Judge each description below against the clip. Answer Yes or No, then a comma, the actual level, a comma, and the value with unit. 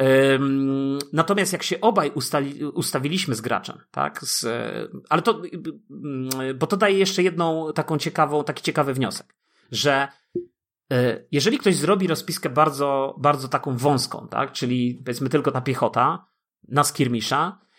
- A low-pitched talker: No, medium, 145 Hz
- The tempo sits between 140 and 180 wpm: No, average, 130 wpm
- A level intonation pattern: No, average, 3.6 semitones